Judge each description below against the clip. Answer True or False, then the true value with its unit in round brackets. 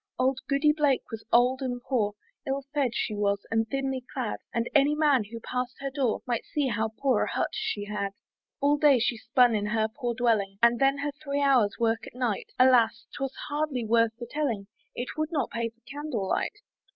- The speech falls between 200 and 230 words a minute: True (205 wpm)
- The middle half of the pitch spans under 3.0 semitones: False (3.5 semitones)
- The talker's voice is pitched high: True (245 Hz)